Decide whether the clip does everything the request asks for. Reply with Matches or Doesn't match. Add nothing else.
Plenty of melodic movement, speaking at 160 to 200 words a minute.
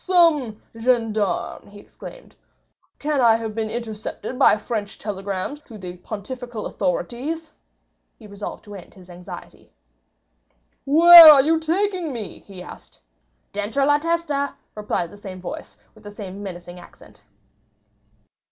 Doesn't match